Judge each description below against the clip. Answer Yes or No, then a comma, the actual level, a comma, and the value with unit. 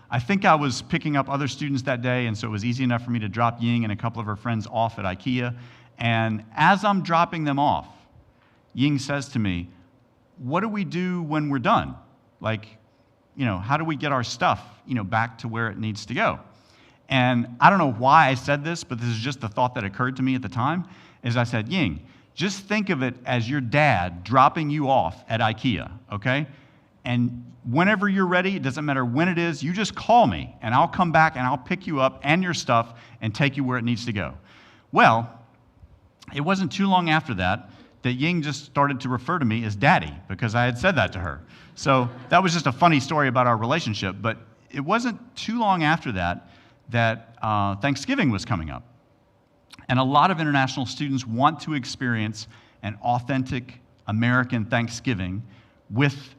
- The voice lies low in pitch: Yes, low, 125 Hz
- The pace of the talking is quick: Yes, fast, 210 wpm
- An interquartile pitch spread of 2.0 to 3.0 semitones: No, average, 4.2 semitones